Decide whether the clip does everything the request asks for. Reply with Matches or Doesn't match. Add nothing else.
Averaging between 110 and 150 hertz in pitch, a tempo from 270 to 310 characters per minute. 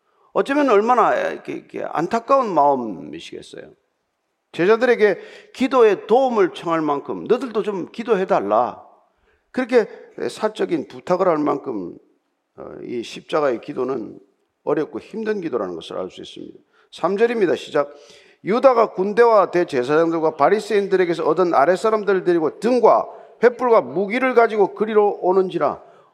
Doesn't match